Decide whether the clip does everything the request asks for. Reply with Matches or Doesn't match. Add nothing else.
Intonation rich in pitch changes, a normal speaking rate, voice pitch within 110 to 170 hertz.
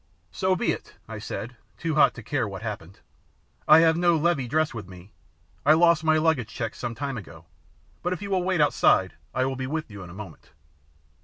Doesn't match